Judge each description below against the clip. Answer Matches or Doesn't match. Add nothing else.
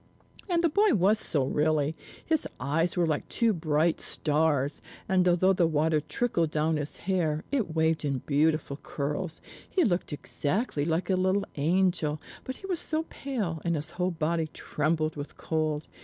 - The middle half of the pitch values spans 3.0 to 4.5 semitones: Matches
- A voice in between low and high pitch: Matches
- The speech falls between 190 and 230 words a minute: Doesn't match